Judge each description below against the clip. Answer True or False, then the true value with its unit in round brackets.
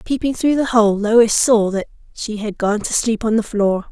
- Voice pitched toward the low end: False (220 Hz)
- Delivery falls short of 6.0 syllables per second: True (4.6 syllables/s)